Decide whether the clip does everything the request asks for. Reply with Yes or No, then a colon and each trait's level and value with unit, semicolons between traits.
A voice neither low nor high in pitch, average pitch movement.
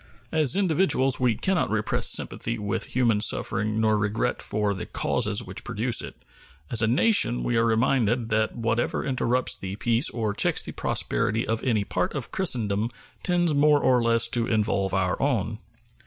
No: low, 115 Hz; average, 3.3 semitones